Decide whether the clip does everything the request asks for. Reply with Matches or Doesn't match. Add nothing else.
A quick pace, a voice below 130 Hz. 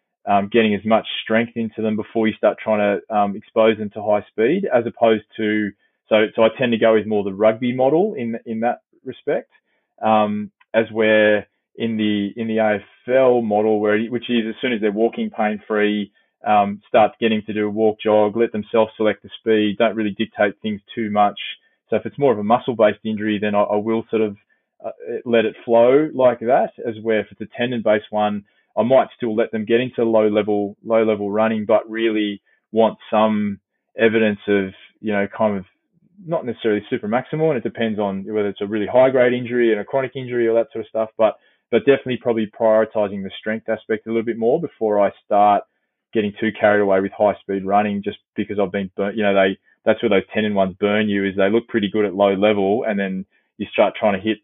Matches